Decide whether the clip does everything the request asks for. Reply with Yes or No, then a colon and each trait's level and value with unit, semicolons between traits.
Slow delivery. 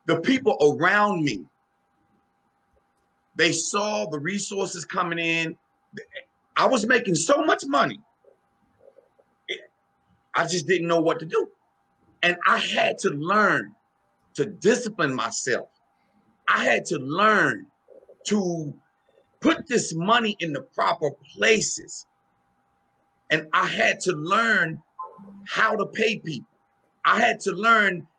Yes: slow, 120 wpm